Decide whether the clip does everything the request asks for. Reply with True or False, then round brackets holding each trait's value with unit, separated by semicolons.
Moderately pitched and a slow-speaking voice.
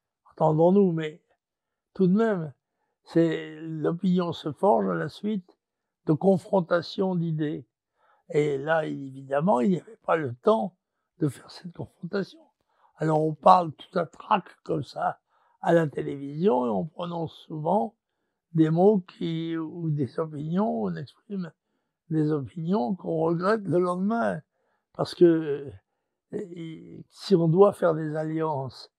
True (170 Hz; 140 wpm)